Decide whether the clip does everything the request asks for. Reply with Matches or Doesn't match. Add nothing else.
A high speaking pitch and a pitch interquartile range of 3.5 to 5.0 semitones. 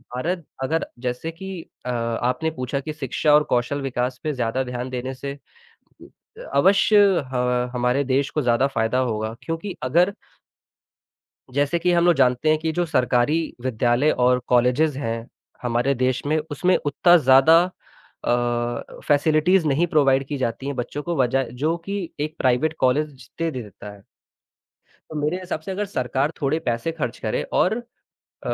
Doesn't match